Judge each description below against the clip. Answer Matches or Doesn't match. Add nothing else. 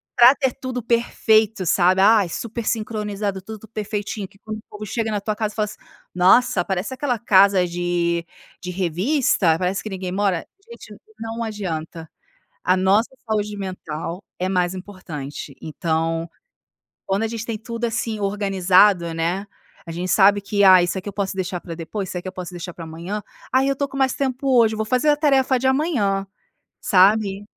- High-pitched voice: Matches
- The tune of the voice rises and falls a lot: Doesn't match